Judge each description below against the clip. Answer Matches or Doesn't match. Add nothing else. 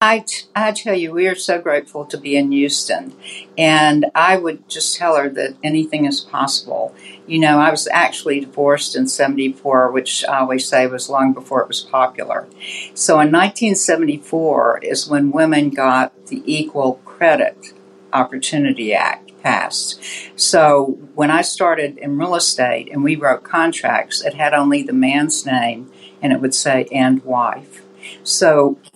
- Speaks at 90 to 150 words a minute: Doesn't match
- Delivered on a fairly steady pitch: Doesn't match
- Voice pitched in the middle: Matches